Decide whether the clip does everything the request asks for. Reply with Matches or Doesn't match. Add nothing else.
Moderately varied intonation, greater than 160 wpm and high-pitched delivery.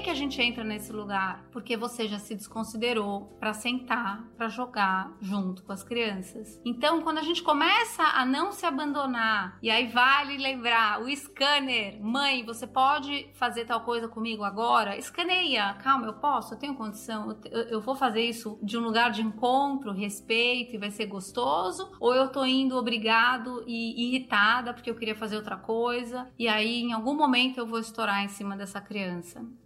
Matches